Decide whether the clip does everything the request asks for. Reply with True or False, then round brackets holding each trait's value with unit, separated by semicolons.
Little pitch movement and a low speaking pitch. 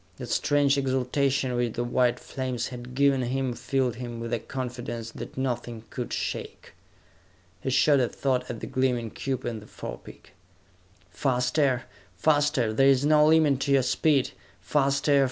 True (2.3 semitones; 130 Hz)